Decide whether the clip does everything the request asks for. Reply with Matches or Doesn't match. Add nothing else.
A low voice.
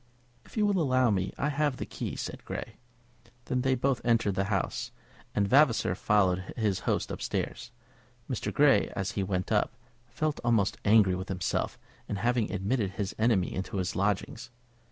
Matches